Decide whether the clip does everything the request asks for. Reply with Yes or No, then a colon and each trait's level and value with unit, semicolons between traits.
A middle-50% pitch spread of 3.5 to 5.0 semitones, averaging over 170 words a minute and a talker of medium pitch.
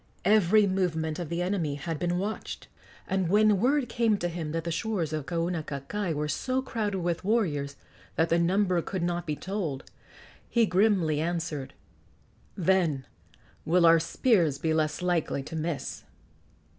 No: average, 3.9 semitones; average, 155 wpm; medium, 175 Hz